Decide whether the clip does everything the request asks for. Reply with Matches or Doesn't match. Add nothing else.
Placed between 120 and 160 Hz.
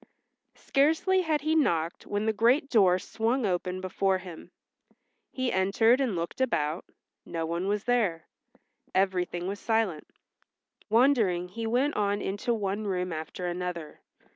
Doesn't match